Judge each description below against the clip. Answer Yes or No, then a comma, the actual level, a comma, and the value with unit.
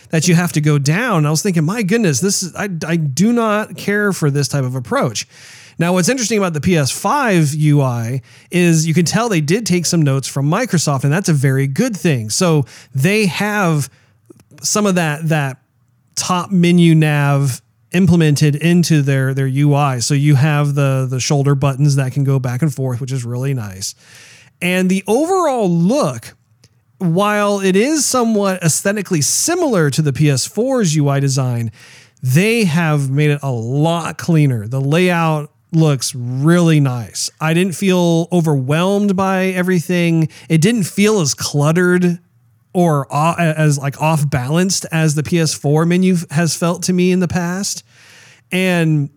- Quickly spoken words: No, average, 160 wpm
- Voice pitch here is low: No, medium, 155 Hz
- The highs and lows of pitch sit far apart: No, average, 4.6 semitones